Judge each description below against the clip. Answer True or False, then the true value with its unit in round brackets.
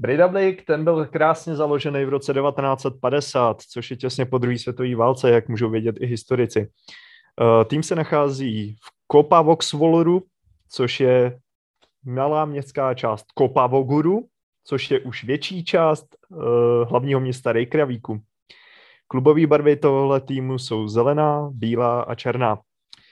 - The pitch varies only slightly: False (3.9 semitones)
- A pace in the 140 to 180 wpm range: False (125 wpm)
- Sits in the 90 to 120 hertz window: False (135 Hz)